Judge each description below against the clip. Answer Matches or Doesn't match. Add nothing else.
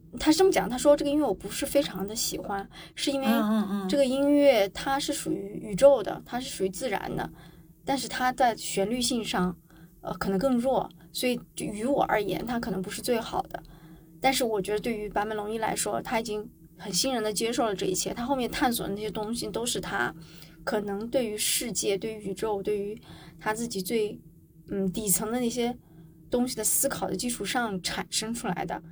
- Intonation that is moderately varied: Matches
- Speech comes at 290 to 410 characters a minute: Matches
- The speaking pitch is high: Matches